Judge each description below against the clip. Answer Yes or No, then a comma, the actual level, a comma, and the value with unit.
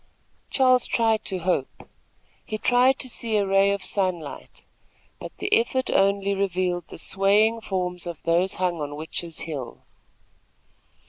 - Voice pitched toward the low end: No, high, 195 Hz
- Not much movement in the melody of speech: No, average, 4.0 semitones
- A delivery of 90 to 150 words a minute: Yes, average, 140 wpm